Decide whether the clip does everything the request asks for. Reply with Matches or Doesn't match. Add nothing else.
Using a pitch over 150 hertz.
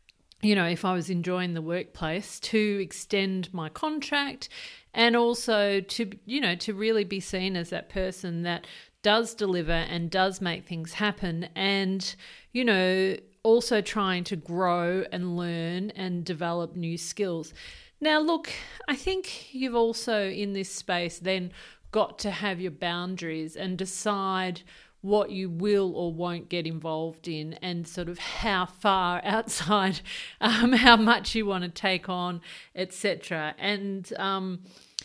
Matches